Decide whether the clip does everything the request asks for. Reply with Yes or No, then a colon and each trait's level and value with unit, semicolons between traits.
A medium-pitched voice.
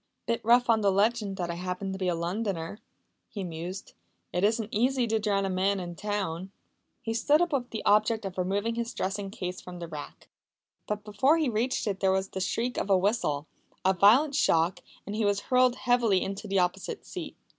No: high, 200 Hz